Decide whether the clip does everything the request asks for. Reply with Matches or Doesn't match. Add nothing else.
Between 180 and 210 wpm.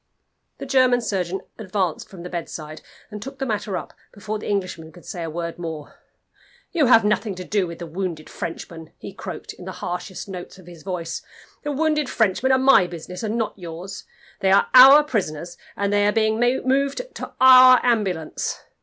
Matches